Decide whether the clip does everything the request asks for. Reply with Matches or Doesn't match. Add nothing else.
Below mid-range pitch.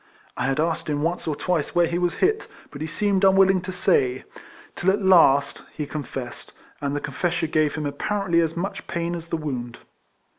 Doesn't match